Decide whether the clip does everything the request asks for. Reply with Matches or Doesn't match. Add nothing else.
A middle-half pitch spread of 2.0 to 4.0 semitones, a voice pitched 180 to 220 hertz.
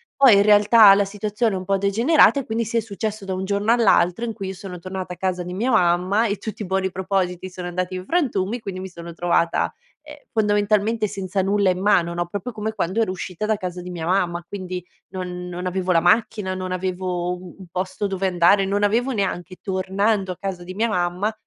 Matches